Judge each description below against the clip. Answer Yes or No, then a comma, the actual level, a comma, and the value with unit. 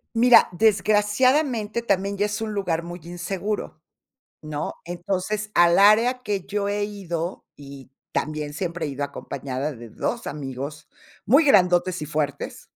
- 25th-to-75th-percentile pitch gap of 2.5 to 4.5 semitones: No, average, 5.3 semitones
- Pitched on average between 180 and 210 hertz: Yes, medium, 185 Hz